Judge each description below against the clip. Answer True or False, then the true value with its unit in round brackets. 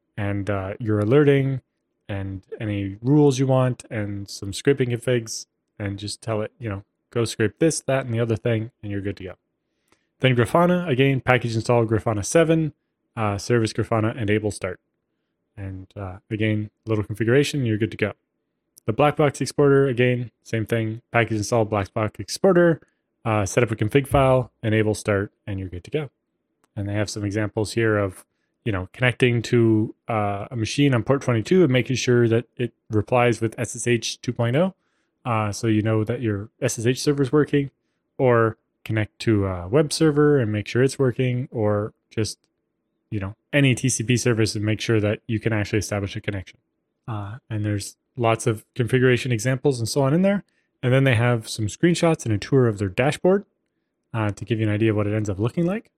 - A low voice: True (115 Hz)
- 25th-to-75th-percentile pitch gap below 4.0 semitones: True (3.5 semitones)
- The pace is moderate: True (195 wpm)